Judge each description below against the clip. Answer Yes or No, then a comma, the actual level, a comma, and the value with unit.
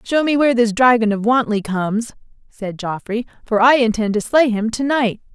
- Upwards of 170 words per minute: Yes, average, 200 wpm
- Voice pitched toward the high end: Yes, high, 230 Hz